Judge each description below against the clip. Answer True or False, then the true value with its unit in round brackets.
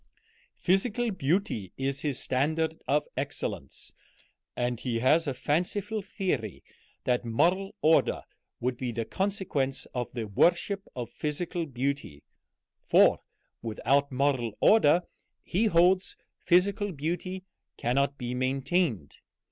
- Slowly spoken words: True (115 wpm)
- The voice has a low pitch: False (145 Hz)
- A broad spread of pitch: True (6.3 semitones)